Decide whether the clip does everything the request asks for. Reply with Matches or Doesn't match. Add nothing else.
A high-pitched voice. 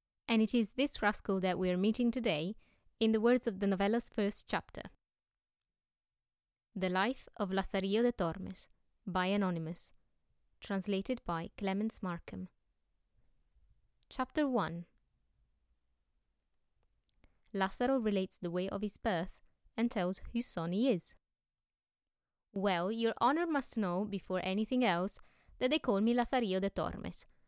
Matches